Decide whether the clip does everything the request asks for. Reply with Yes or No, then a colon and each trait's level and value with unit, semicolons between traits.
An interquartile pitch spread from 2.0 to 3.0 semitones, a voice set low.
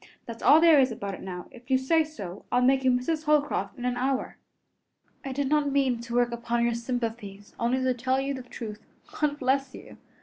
No: narrow, 2.6 semitones; very high, 255 Hz